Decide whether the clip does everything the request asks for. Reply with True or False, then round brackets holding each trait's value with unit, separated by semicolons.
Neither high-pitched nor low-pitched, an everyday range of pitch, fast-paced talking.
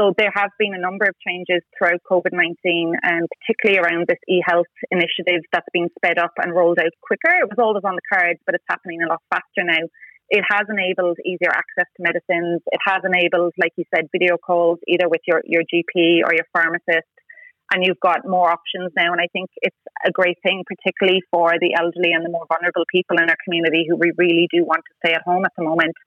False (175 Hz; 1.6 semitones; 230 wpm)